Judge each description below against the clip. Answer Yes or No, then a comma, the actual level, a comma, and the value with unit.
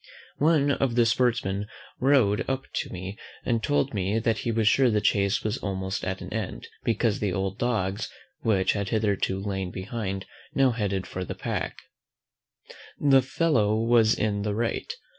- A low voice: Yes, low, 110 Hz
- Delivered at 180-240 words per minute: No, average, 160 wpm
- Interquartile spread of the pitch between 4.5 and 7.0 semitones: No, average, 3.7 semitones